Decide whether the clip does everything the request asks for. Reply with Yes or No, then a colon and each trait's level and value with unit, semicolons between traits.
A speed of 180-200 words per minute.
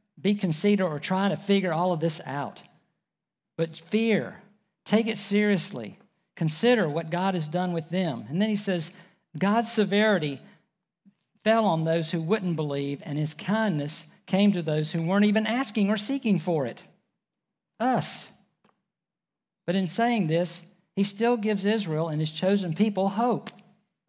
No: average, 155 wpm